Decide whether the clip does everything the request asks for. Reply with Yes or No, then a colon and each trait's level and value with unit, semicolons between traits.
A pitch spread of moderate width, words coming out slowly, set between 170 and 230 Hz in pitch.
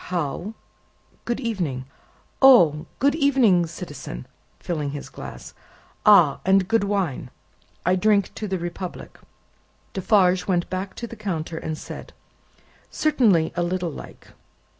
Yes: average, 4.4 semitones; slow, 125 wpm; medium, 185 Hz